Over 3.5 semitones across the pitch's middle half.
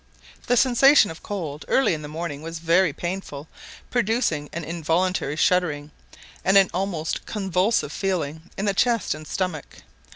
Yes: average, 4.1 semitones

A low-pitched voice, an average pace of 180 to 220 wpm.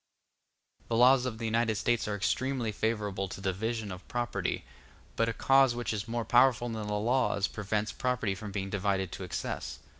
Yes: low, 110 Hz; average, 185 wpm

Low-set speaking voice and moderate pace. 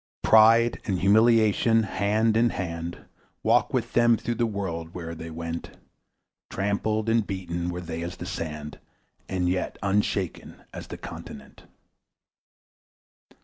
No: very low, 95 Hz; slow, 130 wpm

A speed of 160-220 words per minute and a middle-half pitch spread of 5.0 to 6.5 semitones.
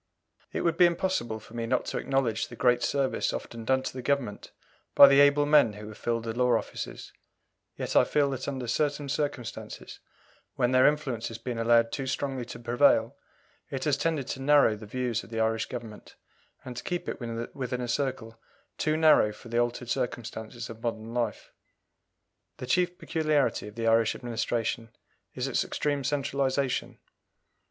No: average, 180 wpm; average, 3.5 semitones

